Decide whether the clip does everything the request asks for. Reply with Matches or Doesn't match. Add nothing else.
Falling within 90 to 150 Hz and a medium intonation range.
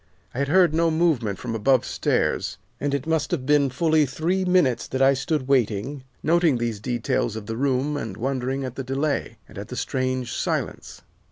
Matches